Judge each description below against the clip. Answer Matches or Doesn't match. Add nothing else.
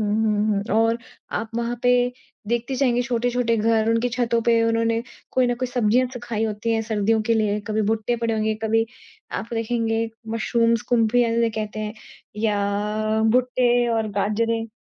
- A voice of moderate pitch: Doesn't match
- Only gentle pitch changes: Matches